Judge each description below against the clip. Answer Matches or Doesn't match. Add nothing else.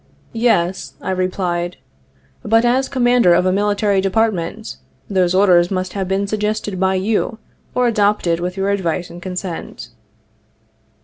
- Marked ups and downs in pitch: Doesn't match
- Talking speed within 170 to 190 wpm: Doesn't match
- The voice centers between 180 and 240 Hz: Matches